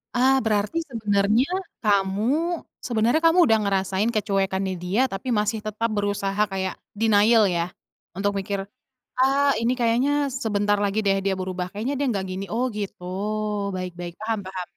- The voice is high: Yes, high, 205 Hz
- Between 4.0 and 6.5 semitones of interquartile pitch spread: No, average, 2.8 semitones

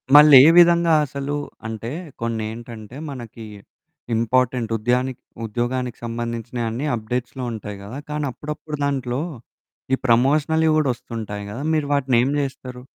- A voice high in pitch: No, low, 125 Hz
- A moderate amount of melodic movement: Yes, average, 3.4 semitones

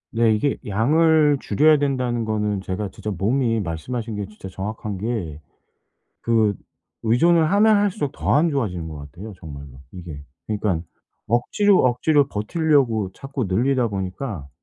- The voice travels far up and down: Yes, wide, 6.3 semitones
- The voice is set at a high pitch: No, low, 110 Hz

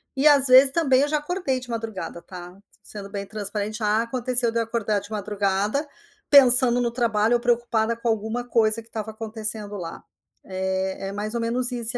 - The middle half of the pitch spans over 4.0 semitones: No, average, 2.9 semitones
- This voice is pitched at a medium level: No, high, 225 Hz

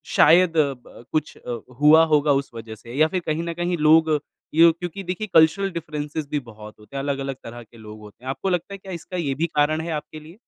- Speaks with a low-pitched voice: No, medium, 155 Hz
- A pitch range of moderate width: Yes, average, 3.6 semitones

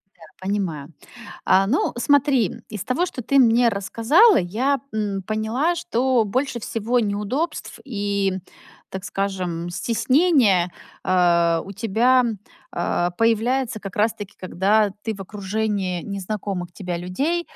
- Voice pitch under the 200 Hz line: No, high, 210 Hz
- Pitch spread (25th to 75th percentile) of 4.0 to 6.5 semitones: Yes, average, 4.6 semitones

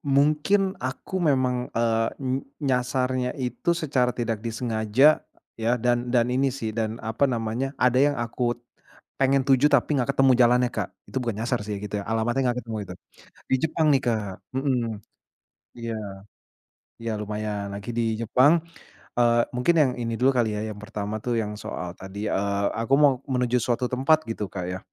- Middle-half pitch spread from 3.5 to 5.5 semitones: No, average, 2.8 semitones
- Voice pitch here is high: No, low, 120 Hz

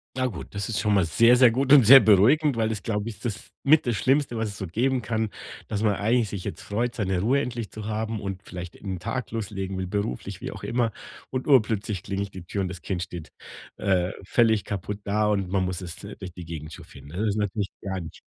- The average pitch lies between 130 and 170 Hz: No, low, 105 Hz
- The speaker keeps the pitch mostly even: No, average, 3.5 semitones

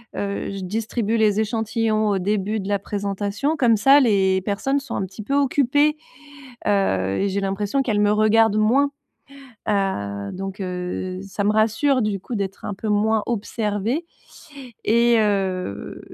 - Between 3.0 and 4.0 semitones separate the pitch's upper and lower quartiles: No, narrow, 2.6 semitones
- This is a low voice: No, high, 210 Hz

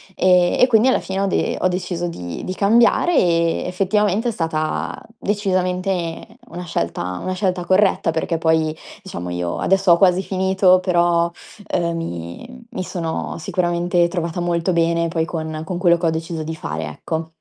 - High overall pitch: No, medium, 175 Hz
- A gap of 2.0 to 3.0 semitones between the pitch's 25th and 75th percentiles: Yes, narrow, 2.4 semitones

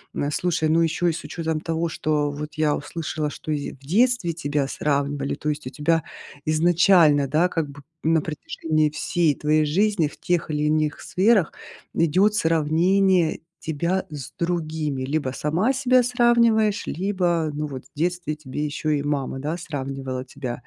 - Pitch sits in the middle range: Yes, medium, 155 Hz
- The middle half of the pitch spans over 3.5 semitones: No, average, 3.0 semitones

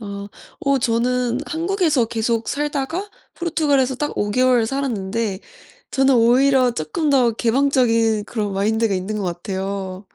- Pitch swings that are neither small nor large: Yes, average, 4.7 semitones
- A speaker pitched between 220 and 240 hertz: Yes, high, 235 Hz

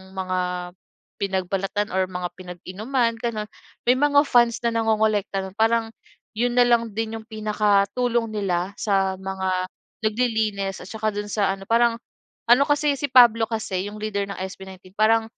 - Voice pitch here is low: No, high, 215 Hz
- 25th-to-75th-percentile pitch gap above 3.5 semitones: No, average, 3.2 semitones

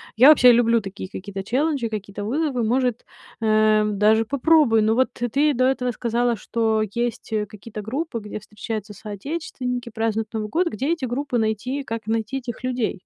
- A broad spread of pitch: No, average, 3.0 semitones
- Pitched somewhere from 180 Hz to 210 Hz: No, high, 230 Hz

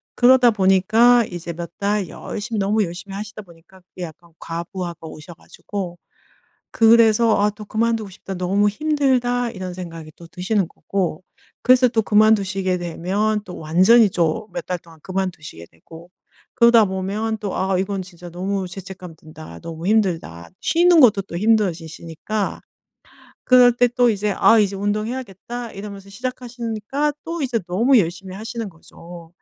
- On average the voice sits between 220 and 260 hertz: No, high, 200 Hz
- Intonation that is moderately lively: Yes, average, 4.1 semitones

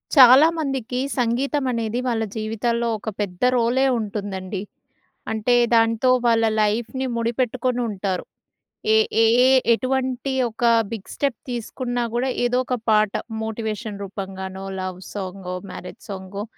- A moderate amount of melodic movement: Yes, average, 3.3 semitones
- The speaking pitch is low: No, high, 230 Hz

